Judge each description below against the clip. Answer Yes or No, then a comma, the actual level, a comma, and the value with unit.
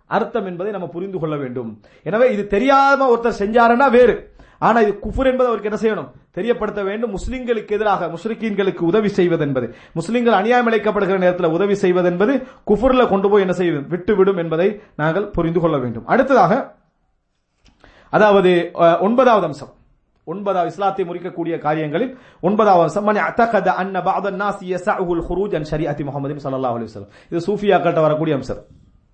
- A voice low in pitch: No, high, 190 Hz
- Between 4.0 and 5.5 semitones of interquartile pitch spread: Yes, average, 4.5 semitones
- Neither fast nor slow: No, slow, 120 wpm